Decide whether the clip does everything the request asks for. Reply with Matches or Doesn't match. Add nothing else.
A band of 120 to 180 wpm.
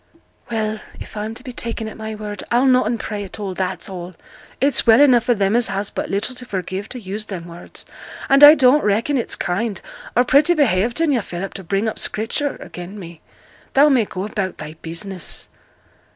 Doesn't match